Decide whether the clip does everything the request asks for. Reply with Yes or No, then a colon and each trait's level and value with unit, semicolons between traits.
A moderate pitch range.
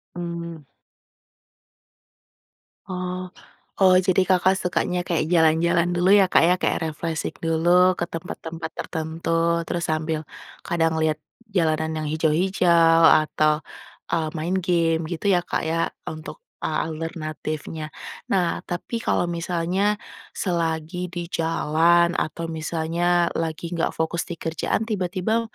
No: narrow, 1.7 semitones